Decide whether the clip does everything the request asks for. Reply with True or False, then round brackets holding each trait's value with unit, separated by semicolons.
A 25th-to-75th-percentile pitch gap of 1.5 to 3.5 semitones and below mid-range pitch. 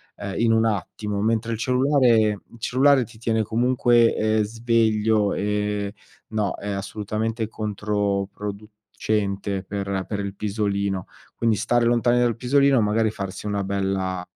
True (2.4 semitones; 105 Hz)